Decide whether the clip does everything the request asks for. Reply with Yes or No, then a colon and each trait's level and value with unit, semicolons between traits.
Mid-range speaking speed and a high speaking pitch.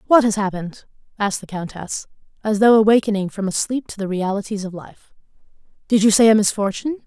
Yes: average, 185 wpm; high, 210 Hz